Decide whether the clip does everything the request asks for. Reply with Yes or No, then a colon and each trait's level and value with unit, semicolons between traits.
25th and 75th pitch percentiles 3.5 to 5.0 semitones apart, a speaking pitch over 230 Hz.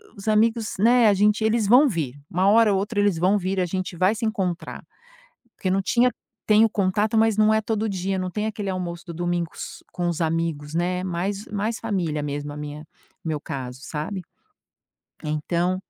No: average, 4.0 semitones; high, 190 Hz